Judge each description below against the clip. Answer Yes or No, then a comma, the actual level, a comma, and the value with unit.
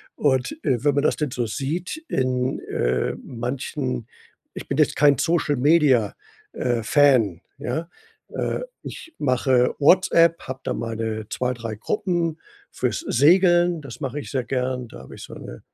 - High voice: No, low, 130 Hz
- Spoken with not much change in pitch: No, average, 4.0 semitones